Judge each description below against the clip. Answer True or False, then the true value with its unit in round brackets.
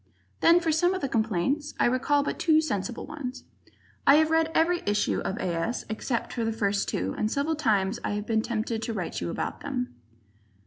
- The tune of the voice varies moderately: False (6.8 semitones)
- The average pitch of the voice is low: False (235 Hz)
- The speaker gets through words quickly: True (210 wpm)